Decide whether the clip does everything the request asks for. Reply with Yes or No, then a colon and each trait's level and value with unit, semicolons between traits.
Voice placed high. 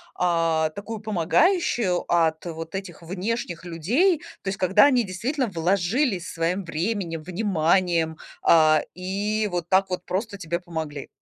No: medium, 180 Hz